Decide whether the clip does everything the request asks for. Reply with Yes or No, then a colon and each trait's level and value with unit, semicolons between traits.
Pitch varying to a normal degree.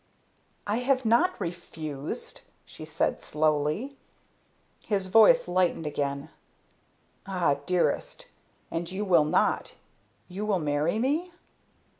No: wide, 6.5 semitones